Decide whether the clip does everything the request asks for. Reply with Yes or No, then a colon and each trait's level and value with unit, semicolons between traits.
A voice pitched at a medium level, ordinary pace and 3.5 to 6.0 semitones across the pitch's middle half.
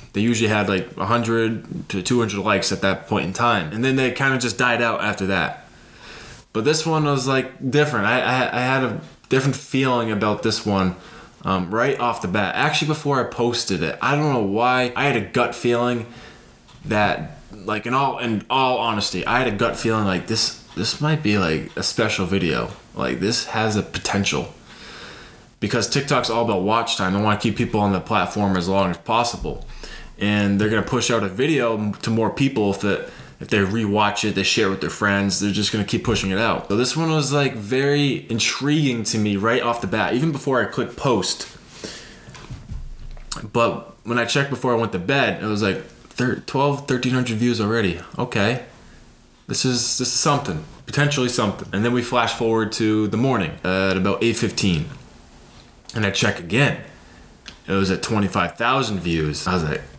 No: low, 115 Hz; average, 195 wpm; average, 3.9 semitones